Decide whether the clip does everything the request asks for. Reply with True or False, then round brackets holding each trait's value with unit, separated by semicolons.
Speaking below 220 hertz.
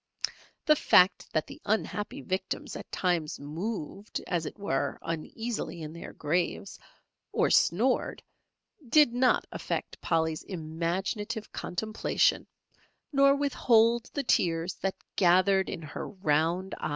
True (190 Hz)